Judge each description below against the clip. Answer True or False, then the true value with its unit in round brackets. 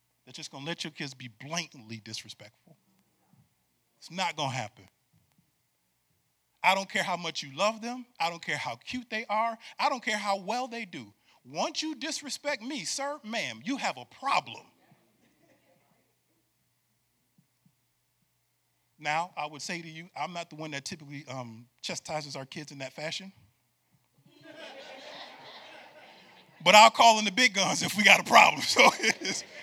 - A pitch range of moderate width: False (8.3 semitones)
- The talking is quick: False (160 wpm)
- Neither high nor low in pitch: True (170 Hz)